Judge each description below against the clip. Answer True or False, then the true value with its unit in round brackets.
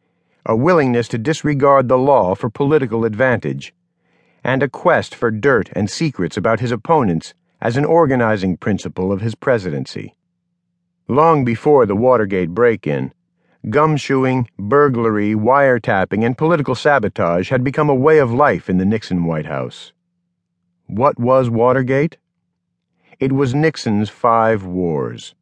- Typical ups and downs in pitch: False (5.8 semitones)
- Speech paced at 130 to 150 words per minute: True (135 wpm)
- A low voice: True (130 Hz)